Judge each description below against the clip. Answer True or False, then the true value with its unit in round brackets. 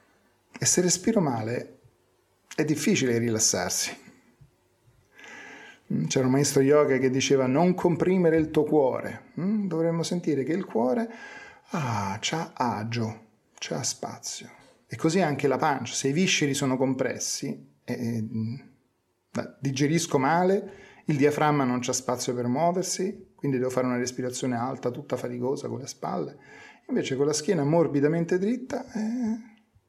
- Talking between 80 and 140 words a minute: True (135 wpm)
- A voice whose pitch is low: False (145 Hz)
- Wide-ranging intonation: True (6.0 semitones)